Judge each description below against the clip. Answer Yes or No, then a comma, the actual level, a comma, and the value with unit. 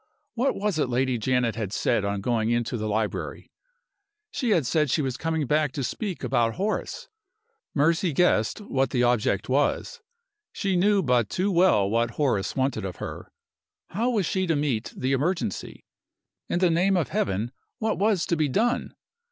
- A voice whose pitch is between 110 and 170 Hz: Yes, medium, 140 Hz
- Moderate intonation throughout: No, wide, 7.5 semitones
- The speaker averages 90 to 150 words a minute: No, average, 175 wpm